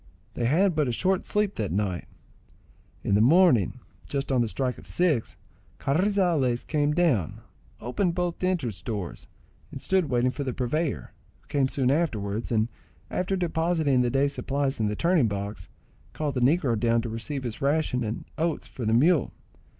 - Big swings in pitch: Yes, wide, 6.2 semitones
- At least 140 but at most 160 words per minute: No, average, 175 wpm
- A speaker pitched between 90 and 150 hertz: Yes, low, 135 Hz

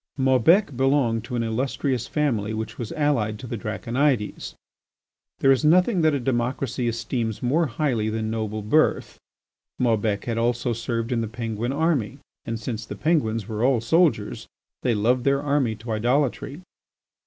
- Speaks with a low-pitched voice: Yes, low, 120 Hz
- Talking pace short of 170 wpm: Yes, average, 155 wpm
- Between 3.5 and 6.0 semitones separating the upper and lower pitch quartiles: Yes, average, 3.8 semitones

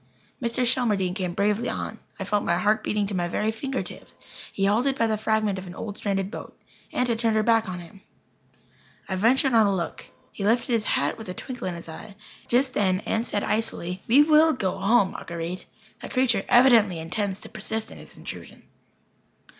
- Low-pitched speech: No, high, 210 Hz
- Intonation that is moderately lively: Yes, average, 3.6 semitones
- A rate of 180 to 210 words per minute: Yes, average, 200 wpm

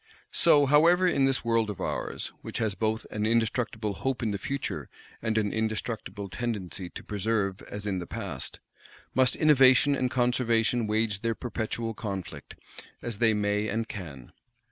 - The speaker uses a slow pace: No, average, 160 wpm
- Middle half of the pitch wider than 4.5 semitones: No, average, 3.0 semitones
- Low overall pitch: Yes, low, 110 Hz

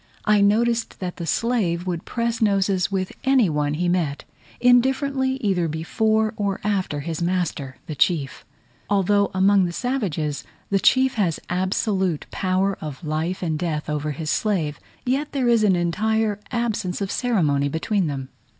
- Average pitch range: Yes, average, 5.0 semitones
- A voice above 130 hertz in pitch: Yes, high, 190 Hz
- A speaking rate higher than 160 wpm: No, average, 155 wpm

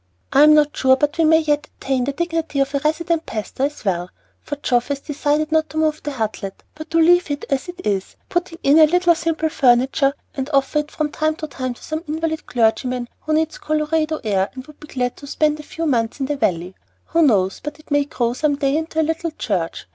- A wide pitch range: No, average, 3.3 semitones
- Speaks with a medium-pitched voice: No, very high, 295 Hz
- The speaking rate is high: Yes, fast, 235 wpm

